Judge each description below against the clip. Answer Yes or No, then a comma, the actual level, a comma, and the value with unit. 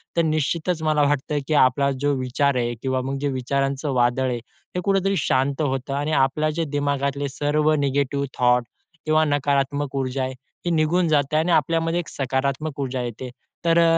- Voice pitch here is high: No, medium, 140 Hz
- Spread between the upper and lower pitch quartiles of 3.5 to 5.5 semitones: No, average, 2.7 semitones